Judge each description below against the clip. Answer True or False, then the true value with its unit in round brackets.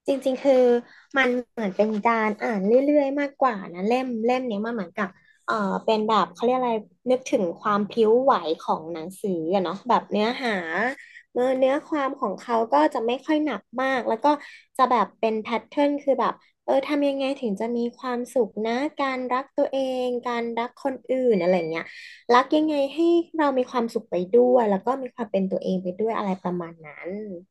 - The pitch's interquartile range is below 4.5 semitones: True (4.1 semitones)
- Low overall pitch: False (245 Hz)